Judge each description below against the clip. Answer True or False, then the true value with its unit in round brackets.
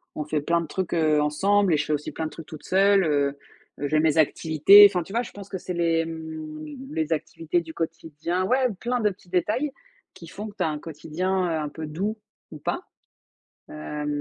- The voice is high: False (165 Hz)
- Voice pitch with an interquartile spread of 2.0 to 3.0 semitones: False (3.6 semitones)